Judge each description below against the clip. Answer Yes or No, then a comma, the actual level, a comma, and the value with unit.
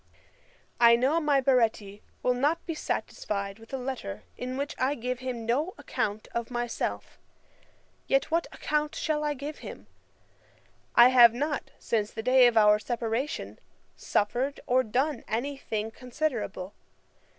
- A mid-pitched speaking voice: No, very high, 250 Hz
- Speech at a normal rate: Yes, average, 150 wpm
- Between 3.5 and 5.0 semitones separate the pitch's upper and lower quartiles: Yes, average, 3.9 semitones